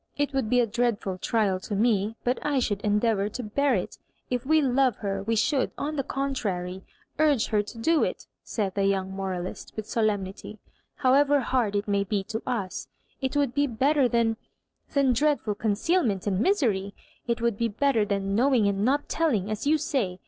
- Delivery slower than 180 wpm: No, average, 190 wpm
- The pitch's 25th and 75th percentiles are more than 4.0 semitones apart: Yes, average, 5.1 semitones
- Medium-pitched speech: No, high, 225 Hz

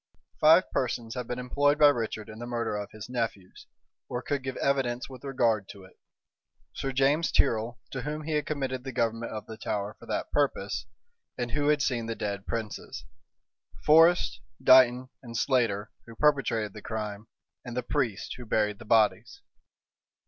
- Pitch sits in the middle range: No, low, 120 Hz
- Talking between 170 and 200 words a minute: Yes, average, 175 wpm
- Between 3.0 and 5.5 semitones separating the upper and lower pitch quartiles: Yes, average, 3.7 semitones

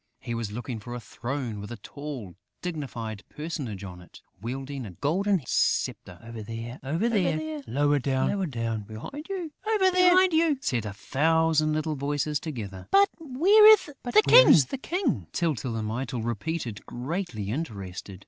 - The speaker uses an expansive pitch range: Yes, wide, 7.7 semitones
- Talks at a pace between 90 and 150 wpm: Yes, average, 140 wpm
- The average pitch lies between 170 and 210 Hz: No, medium, 140 Hz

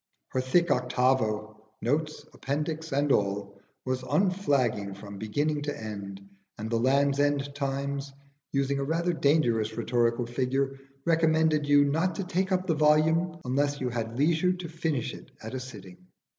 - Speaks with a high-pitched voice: No, medium, 140 Hz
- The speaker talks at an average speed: Yes, average, 155 wpm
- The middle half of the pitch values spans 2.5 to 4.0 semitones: No, average, 4.6 semitones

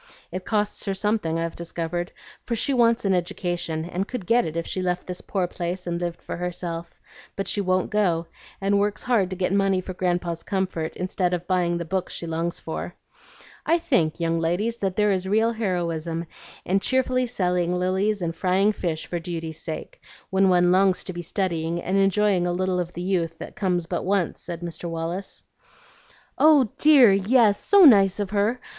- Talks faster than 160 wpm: Yes, average, 190 wpm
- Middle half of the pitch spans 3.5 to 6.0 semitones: No, average, 2.8 semitones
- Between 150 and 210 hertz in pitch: Yes, medium, 185 Hz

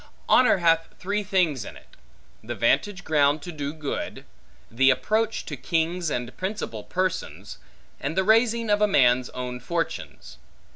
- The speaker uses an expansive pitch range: Yes, wide, 7.1 semitones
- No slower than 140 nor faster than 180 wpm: Yes, average, 150 wpm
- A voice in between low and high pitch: Yes, medium, 165 Hz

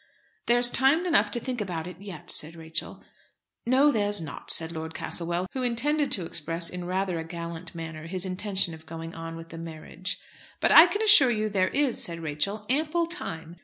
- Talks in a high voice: No, medium, 180 Hz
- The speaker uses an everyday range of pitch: No, wide, 6.6 semitones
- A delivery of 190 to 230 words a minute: Yes, average, 195 wpm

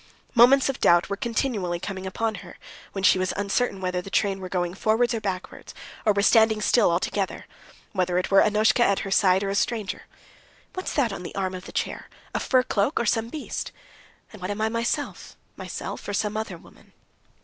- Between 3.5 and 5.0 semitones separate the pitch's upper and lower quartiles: No, average, 3.1 semitones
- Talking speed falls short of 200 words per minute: No, fast, 205 wpm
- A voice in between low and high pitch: No, high, 205 Hz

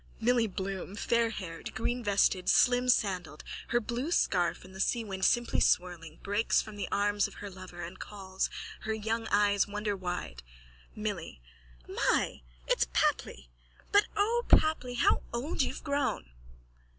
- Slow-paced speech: Yes, slow, 130 wpm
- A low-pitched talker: No, high, 205 Hz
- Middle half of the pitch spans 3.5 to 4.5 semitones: Yes, average, 4.2 semitones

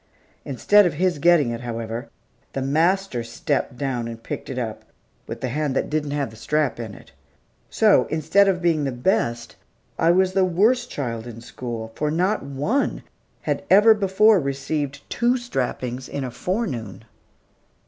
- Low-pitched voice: No, medium, 145 Hz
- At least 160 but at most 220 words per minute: Yes, average, 165 wpm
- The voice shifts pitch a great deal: Yes, wide, 7.4 semitones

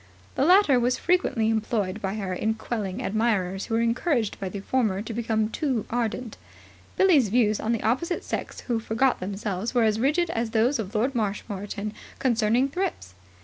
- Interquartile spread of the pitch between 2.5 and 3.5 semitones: Yes, average, 3.2 semitones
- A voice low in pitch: No, high, 225 Hz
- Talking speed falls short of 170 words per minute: No, average, 175 wpm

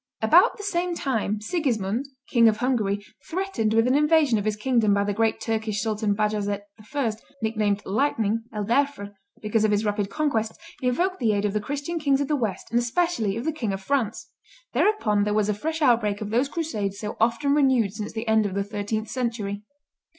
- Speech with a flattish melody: No, average, 4.8 semitones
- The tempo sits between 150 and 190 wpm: No, average, 200 wpm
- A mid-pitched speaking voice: No, high, 225 Hz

